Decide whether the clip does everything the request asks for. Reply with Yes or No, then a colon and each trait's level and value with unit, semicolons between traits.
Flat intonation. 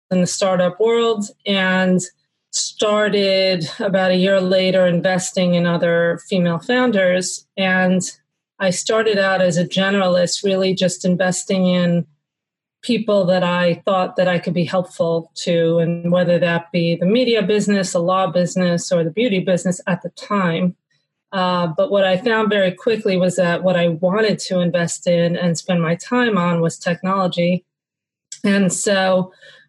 Yes: narrow, 1.9 semitones